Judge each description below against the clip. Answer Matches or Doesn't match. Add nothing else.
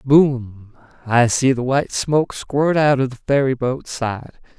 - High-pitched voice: Doesn't match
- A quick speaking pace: Doesn't match